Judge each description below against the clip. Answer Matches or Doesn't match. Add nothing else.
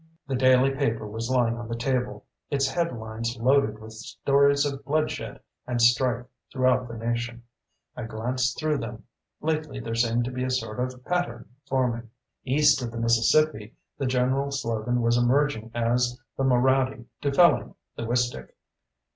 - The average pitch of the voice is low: Matches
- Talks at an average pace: Matches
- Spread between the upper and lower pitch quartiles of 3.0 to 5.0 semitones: Doesn't match